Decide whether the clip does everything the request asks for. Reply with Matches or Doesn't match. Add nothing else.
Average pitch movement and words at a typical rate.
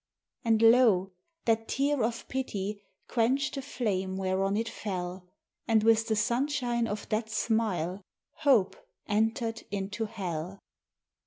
Doesn't match